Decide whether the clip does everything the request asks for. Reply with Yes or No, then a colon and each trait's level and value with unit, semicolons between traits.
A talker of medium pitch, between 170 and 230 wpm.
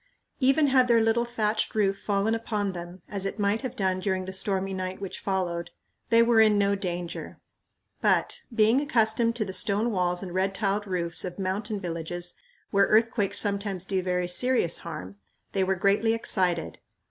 No: high, 200 Hz; average, 175 wpm